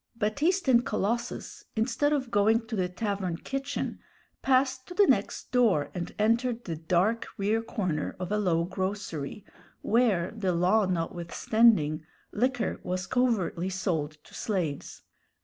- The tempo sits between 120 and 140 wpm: Yes, slow, 135 wpm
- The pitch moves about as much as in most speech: Yes, average, 4.9 semitones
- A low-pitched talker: No, high, 210 Hz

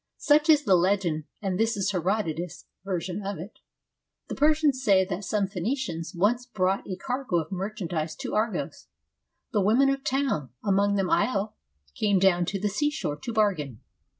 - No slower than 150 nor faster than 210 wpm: Yes, average, 170 wpm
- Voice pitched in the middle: No, high, 200 Hz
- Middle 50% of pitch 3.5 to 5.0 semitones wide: Yes, average, 4.5 semitones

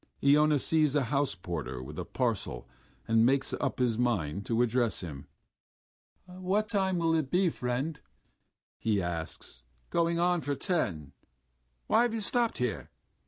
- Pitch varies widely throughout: Yes, wide, 9.0 semitones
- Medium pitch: No, low, 130 Hz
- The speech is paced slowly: No, average, 150 wpm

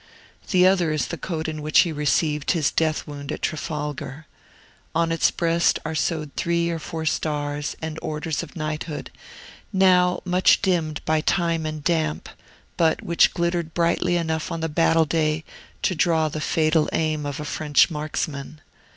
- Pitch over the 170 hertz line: No, medium, 160 Hz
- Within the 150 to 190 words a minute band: Yes, average, 165 wpm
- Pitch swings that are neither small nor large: No, narrow, 1.8 semitones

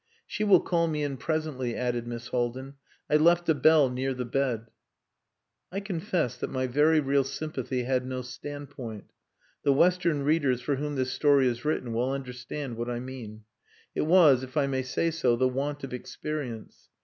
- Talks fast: No, average, 180 wpm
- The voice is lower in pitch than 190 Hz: Yes, low, 135 Hz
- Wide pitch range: No, average, 3.4 semitones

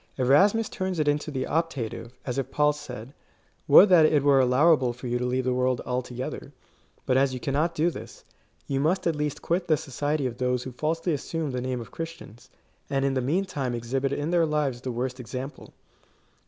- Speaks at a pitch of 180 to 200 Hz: No, low, 135 Hz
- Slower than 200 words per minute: No, fast, 205 wpm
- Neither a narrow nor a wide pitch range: Yes, average, 3.5 semitones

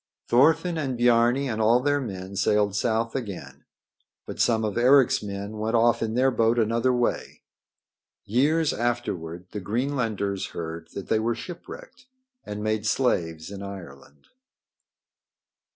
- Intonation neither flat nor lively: Yes, average, 3.8 semitones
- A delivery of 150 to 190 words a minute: No, slow, 135 wpm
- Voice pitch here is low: Yes, low, 115 Hz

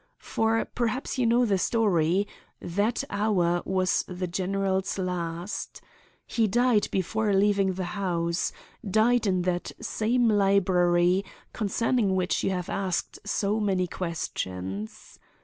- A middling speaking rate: No, slow, 115 wpm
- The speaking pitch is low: No, high, 195 Hz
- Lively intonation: No, average, 3.3 semitones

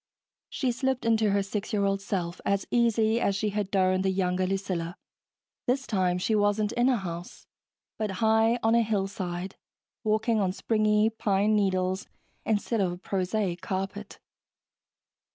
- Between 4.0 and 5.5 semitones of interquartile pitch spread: No, average, 2.7 semitones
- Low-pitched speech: No, high, 200 Hz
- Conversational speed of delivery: Yes, average, 150 wpm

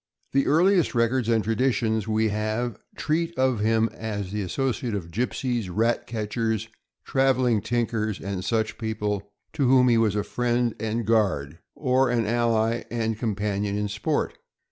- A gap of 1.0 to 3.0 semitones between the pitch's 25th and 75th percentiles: Yes, narrow, 2.5 semitones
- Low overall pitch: Yes, low, 115 Hz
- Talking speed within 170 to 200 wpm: No, average, 150 wpm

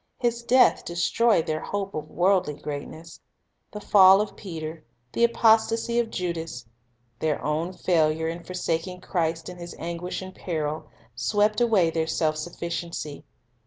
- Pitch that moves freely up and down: No, average, 4.0 semitones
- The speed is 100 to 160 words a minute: Yes, average, 140 wpm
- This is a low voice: No, medium, 175 Hz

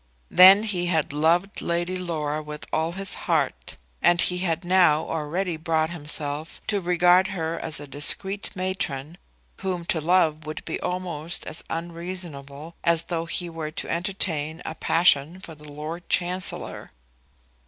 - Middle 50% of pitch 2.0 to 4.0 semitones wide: Yes, average, 2.7 semitones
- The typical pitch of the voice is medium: Yes, medium, 170 Hz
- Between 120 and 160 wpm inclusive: Yes, average, 150 wpm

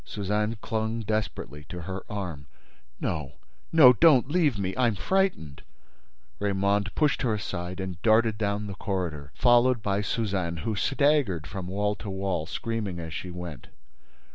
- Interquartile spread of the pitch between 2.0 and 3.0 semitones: No, average, 4.2 semitones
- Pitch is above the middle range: No, low, 100 Hz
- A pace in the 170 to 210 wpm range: No, slow, 135 wpm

